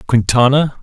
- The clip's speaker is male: Yes, male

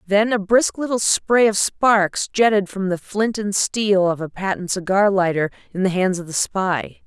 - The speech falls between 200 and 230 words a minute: Yes, fast, 205 wpm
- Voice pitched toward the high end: Yes, high, 195 Hz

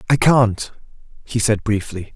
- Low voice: Yes, low, 115 Hz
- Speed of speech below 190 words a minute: Yes, average, 140 wpm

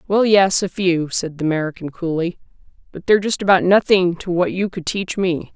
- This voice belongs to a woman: Yes, female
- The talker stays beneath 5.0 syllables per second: No, 5.3 syllables/s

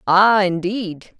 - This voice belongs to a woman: Yes, female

